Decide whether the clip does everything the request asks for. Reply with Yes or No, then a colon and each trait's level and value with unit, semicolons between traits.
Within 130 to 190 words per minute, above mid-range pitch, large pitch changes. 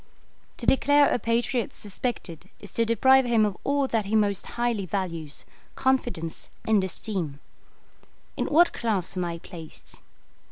No: average, 145 wpm; high, 215 Hz; average, 4.7 semitones